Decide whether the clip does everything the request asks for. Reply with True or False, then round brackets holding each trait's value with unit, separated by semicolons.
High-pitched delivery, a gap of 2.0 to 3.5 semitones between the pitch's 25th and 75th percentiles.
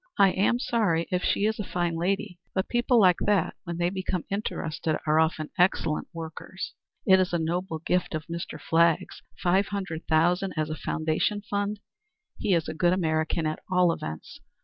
False (175 Hz; 3.2 semitones)